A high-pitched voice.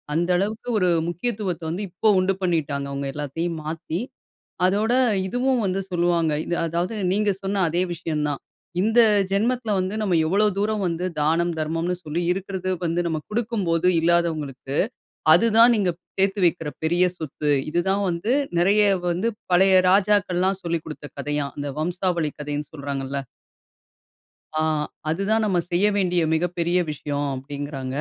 No: medium, 175 Hz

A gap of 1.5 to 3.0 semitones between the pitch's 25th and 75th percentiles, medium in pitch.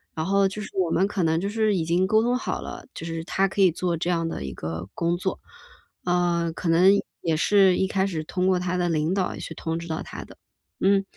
Yes: average, 2.7 semitones; medium, 180 Hz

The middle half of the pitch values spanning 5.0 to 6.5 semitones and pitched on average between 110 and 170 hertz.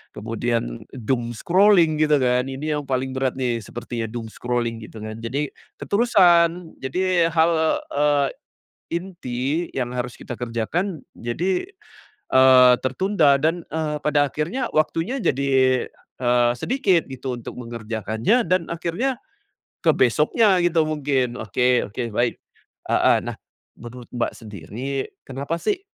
Yes: wide, 5.6 semitones; low, 135 Hz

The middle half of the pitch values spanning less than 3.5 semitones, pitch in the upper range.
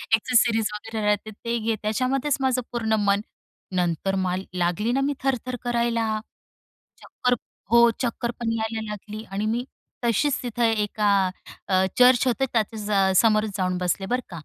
Yes: average, 2.9 semitones; high, 220 Hz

